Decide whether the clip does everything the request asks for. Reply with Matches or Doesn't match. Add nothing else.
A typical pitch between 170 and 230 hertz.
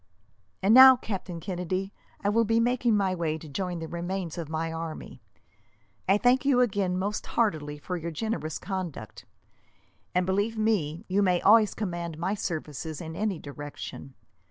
Matches